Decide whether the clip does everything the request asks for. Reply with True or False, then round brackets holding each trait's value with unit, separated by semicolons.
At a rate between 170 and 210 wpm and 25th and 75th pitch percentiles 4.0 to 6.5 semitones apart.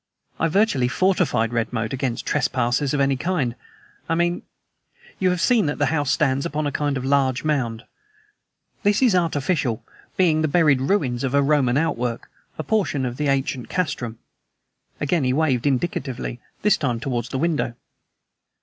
False (160 wpm; 4.6 semitones)